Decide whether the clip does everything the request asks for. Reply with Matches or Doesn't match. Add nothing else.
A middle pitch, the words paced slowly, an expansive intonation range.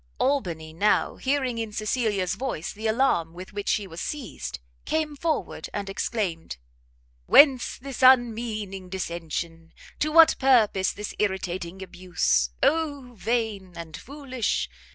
Doesn't match